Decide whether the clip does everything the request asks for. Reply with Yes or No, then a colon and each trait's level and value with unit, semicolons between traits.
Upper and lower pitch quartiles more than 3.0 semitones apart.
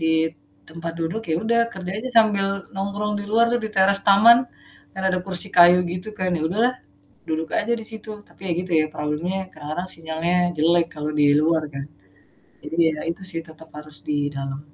Yes: average, 4.0 semitones